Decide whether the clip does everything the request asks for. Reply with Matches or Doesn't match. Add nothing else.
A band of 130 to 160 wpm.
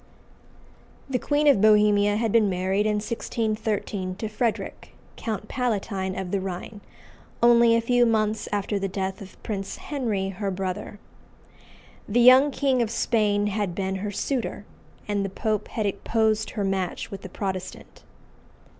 Matches